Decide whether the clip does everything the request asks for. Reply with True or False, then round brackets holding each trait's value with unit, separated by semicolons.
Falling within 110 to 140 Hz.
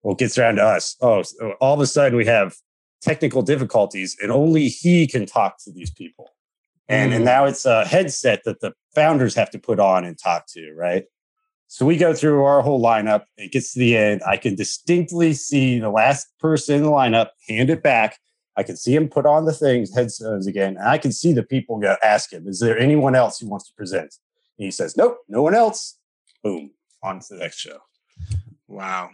True (135 Hz)